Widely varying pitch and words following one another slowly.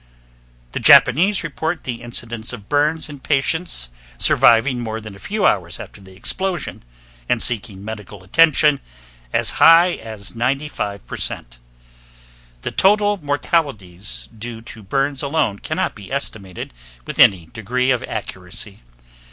Yes: wide, 6.3 semitones; slow, 125 wpm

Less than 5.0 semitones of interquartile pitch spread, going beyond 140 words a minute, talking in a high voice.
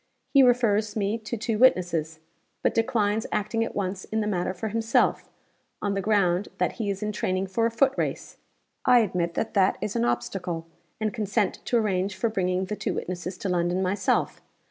Yes: average, 3.3 semitones; average, 190 wpm; high, 205 Hz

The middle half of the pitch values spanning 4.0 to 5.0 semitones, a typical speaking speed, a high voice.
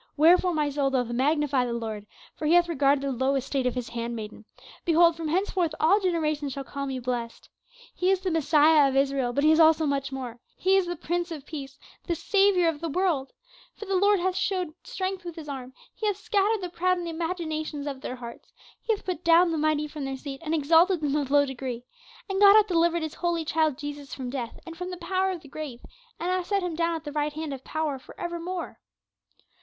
No: average, 4.3 semitones; fast, 235 wpm; very high, 315 Hz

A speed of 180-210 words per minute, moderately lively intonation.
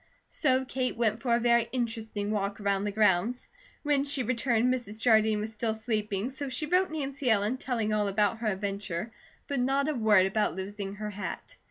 Yes: average, 190 wpm; average, 3.6 semitones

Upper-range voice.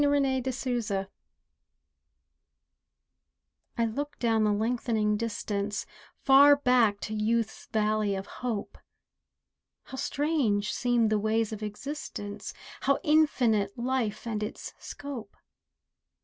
Yes: high, 225 Hz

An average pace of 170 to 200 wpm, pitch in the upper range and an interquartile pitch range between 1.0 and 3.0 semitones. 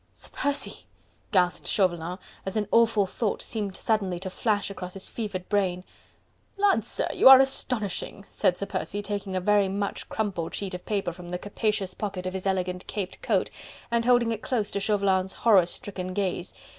Yes: average, 180 wpm; high, 200 Hz; narrow, 2.6 semitones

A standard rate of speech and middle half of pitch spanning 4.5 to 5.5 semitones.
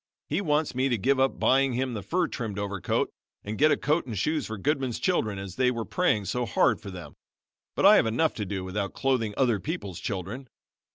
No: fast, 220 wpm; average, 5.2 semitones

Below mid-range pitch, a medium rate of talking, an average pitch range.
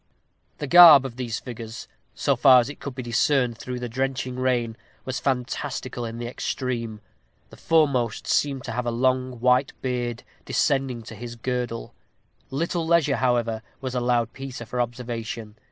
No: low, 125 Hz; average, 160 wpm; narrow, 2.1 semitones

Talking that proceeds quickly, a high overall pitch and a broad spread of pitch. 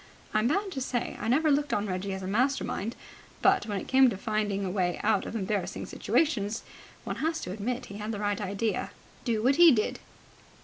No: fast, 215 wpm; high, 215 Hz; average, 4.8 semitones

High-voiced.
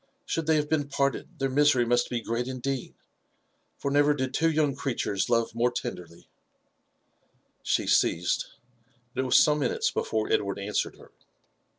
No: low, 135 Hz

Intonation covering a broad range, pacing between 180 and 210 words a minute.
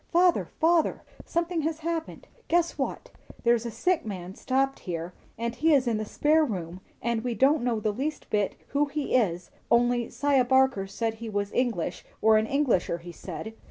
Yes: wide, 5.8 semitones; average, 185 wpm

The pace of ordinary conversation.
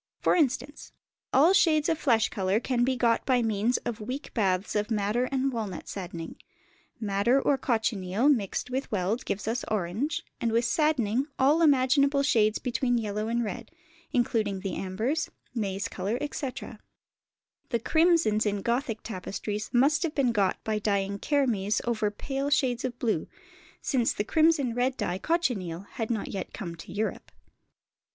Yes: average, 160 wpm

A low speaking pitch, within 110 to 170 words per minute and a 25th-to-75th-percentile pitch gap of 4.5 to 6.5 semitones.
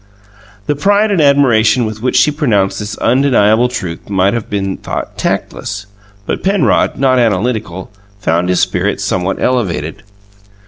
Yes: low, 110 Hz; average, 140 wpm; average, 5.3 semitones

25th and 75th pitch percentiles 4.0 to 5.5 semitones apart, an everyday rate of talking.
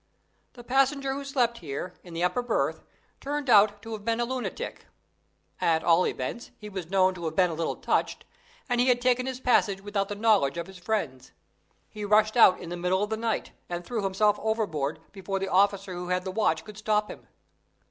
No: average, 4.4 semitones; fast, 210 wpm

